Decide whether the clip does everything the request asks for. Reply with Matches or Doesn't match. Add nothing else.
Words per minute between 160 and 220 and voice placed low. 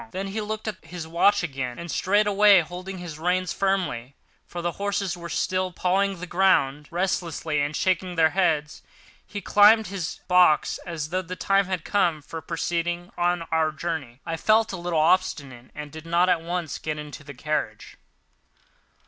Doesn't match